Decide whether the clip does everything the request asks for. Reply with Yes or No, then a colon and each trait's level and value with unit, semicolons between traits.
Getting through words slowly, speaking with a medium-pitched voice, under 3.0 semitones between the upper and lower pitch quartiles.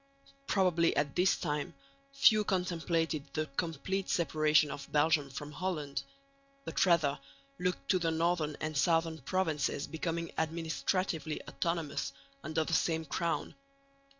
Yes: slow, 125 wpm; medium, 165 Hz; narrow, 2.5 semitones